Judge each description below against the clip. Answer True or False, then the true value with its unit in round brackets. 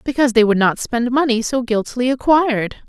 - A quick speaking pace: False (190 wpm)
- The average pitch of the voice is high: True (245 Hz)